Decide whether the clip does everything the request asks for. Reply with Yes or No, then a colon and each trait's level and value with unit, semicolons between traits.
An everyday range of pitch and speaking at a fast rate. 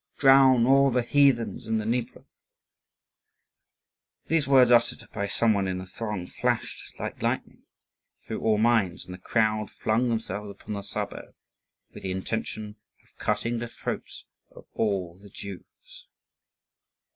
No: average, 3.2 semitones; average, 145 wpm